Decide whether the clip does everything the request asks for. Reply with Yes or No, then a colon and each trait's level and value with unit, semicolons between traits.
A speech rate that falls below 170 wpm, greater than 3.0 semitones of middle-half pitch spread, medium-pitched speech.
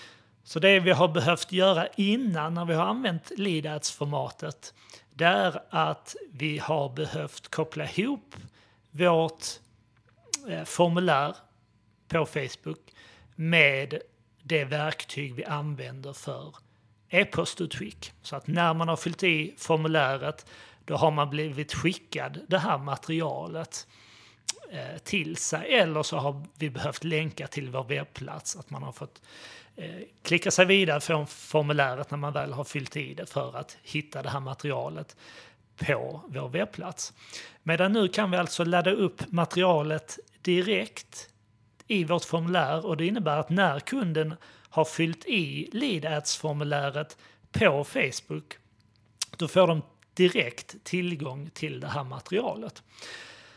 Yes: average, 130 wpm; average, 3.6 semitones; medium, 155 Hz